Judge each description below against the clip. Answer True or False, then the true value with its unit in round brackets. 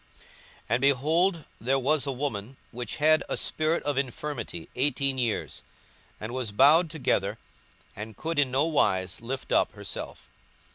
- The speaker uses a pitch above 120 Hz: True (135 Hz)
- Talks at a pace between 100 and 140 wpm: False (150 wpm)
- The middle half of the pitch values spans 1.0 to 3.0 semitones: False (4.4 semitones)